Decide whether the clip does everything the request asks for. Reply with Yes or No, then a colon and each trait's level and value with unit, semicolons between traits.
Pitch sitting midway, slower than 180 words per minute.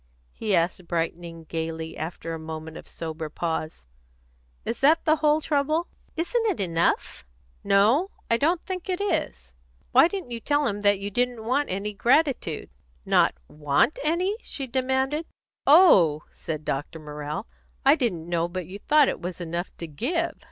No: high, 200 Hz; average, 160 wpm